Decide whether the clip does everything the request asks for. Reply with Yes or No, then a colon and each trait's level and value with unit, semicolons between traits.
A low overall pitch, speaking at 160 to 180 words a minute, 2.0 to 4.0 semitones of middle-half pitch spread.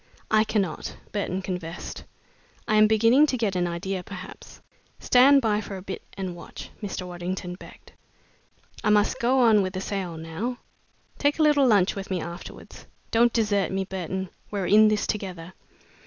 No: high, 195 Hz; average, 170 wpm; average, 3.0 semitones